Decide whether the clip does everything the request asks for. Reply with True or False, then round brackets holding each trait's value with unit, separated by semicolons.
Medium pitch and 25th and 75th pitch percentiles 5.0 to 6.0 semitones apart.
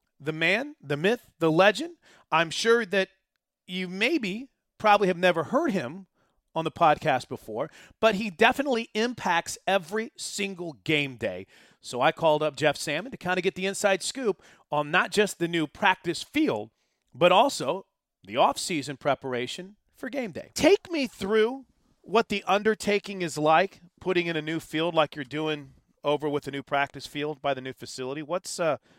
True (175 Hz; 5.3 semitones)